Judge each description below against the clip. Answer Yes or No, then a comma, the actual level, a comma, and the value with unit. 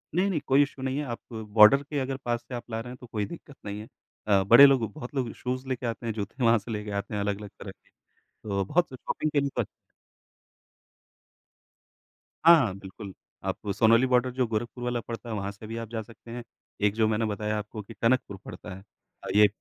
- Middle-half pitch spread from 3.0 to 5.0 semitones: Yes, average, 3.5 semitones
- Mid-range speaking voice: No, low, 115 Hz